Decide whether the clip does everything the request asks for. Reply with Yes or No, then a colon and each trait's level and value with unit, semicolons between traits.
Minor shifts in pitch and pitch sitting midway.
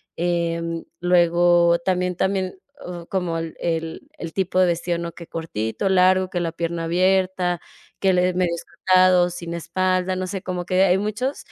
Yes: narrow, 1.6 semitones; medium, 180 Hz